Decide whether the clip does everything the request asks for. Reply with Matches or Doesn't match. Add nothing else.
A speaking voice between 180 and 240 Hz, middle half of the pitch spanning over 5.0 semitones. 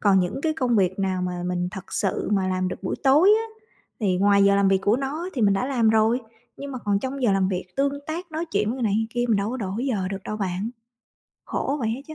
Matches